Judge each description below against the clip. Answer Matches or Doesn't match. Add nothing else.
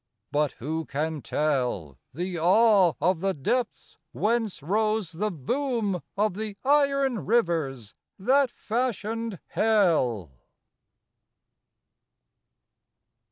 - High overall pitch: Matches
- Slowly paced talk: Matches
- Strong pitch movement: Matches